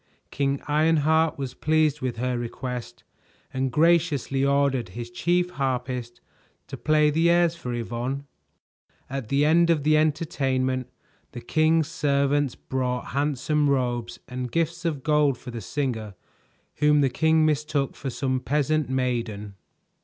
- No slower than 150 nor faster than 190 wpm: No, average, 140 wpm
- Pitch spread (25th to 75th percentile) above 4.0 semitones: No, average, 3.5 semitones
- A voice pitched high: No, medium, 140 Hz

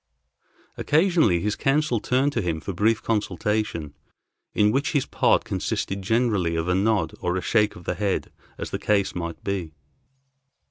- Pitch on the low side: Yes, low, 105 Hz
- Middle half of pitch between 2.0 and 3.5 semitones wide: No, average, 4.5 semitones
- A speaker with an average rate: Yes, average, 160 wpm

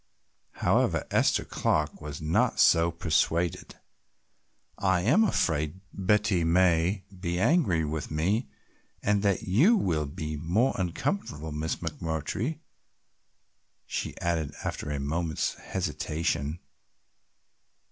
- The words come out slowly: Yes, slow, 105 wpm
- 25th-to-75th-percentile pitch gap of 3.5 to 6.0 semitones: Yes, average, 4.1 semitones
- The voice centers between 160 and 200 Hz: No, very low, 85 Hz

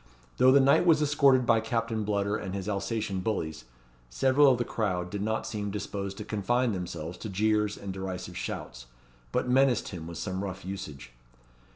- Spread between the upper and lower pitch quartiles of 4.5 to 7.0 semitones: No, average, 3.9 semitones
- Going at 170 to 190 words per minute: Yes, average, 180 wpm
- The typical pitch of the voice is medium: No, low, 105 Hz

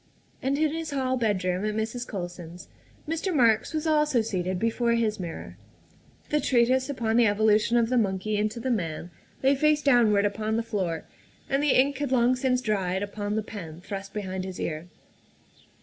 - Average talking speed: Yes, average, 180 wpm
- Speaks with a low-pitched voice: No, high, 220 Hz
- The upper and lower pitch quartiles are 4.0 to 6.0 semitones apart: Yes, average, 4.8 semitones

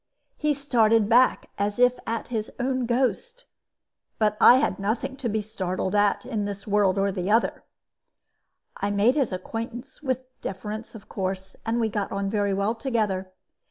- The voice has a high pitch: Yes, high, 220 Hz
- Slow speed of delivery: No, average, 165 wpm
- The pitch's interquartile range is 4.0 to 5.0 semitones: No, average, 3.5 semitones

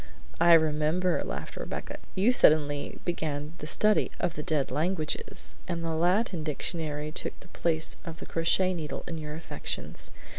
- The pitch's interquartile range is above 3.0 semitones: No, narrow, 2.4 semitones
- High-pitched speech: No, medium, 160 Hz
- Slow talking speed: No, average, 155 wpm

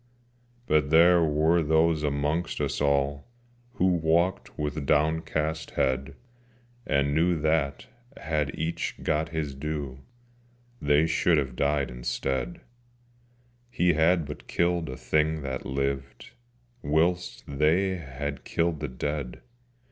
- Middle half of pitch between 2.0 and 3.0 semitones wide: Yes, narrow, 2.5 semitones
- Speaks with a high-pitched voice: No, very low, 75 Hz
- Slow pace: Yes, slow, 120 wpm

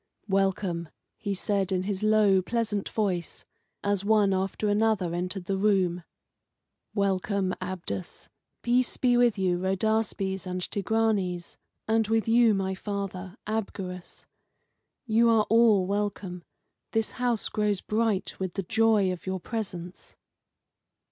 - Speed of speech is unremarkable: No, slow, 125 wpm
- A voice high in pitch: Yes, high, 200 Hz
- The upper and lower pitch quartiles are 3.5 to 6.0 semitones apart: No, average, 2.9 semitones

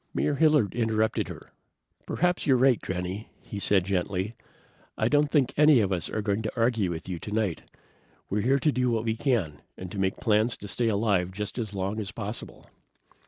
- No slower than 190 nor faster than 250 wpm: Yes, average, 195 wpm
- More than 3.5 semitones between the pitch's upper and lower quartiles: Yes, average, 4.0 semitones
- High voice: No, low, 110 Hz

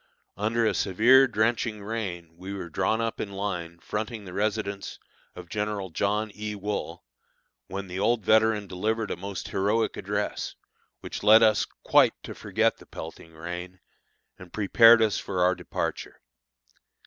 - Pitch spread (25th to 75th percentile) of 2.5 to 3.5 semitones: Yes, average, 3.1 semitones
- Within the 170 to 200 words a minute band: No, average, 150 wpm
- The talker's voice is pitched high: No, low, 100 Hz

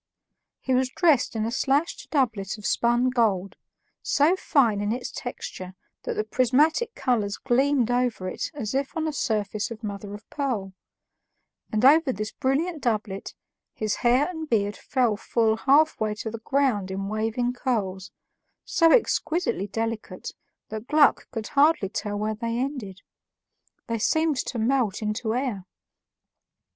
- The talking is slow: No, average, 150 wpm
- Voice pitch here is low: No, high, 235 Hz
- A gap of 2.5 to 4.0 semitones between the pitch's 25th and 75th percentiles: No, average, 4.4 semitones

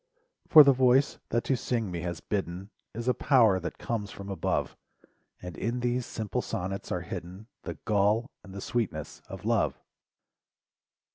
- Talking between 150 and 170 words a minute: Yes, average, 160 wpm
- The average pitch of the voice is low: Yes, low, 105 Hz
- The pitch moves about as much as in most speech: Yes, average, 4.4 semitones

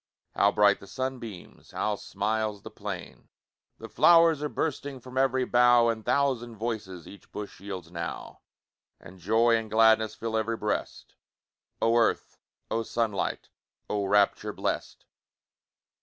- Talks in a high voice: No, low, 110 Hz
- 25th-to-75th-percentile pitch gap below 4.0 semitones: Yes, average, 2.9 semitones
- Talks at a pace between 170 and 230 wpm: No, slow, 135 wpm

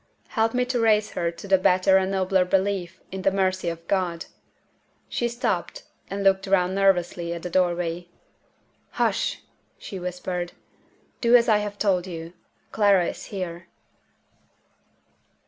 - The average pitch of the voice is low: No, high, 190 Hz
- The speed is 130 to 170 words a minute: Yes, average, 145 wpm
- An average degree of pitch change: No, narrow, 2.2 semitones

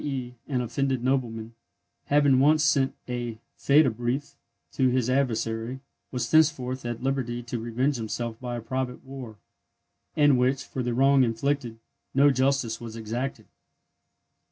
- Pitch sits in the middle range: No, low, 125 Hz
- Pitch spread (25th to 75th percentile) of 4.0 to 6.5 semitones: No, narrow, 2.6 semitones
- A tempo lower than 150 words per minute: Yes, average, 140 wpm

